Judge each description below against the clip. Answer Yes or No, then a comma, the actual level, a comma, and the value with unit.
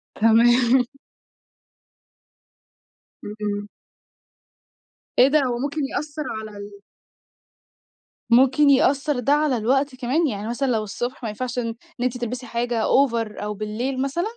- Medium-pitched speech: No, high, 245 Hz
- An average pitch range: Yes, average, 3.5 semitones